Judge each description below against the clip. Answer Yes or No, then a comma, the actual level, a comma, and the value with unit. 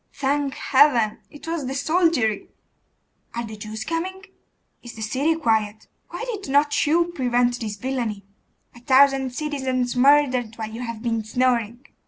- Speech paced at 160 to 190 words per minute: No, average, 150 wpm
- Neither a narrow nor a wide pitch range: Yes, average, 4.2 semitones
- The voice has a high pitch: Yes, very high, 255 Hz